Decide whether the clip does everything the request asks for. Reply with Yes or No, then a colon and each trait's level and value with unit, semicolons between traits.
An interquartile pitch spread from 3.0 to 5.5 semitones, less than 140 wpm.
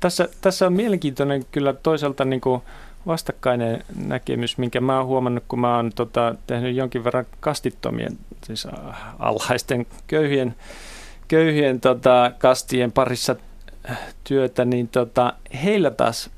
No: narrow, 2.5 semitones; average, 120 wpm